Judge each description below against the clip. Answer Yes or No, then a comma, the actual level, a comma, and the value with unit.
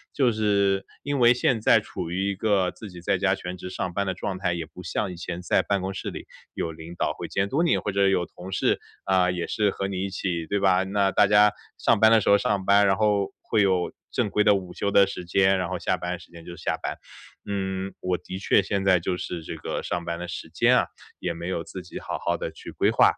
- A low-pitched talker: Yes, very low, 95 Hz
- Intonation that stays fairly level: Yes, narrow, 2.1 semitones